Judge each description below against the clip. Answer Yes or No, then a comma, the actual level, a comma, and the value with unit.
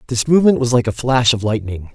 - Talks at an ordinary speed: No, fast, 245 wpm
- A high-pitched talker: No, low, 120 Hz